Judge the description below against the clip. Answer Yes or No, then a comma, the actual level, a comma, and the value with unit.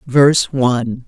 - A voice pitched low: Yes, low, 130 Hz